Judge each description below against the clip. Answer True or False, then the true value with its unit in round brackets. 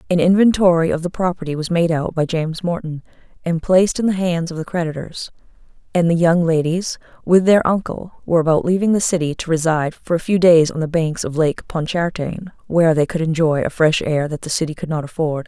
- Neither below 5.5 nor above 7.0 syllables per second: True (5.8 syllables/s)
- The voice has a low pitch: False (165 Hz)